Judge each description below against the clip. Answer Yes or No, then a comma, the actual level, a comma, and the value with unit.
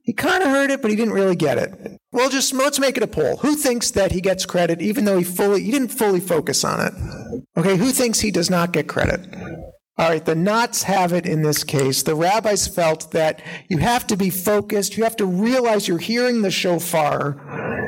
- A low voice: No, high, 195 Hz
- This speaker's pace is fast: Yes, fast, 220 wpm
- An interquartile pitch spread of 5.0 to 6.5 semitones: Yes, wide, 5.5 semitones